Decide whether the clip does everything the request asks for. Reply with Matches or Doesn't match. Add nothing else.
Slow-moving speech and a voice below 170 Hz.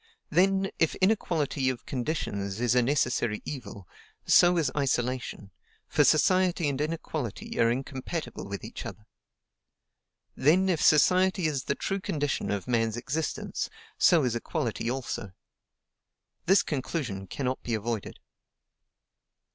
Matches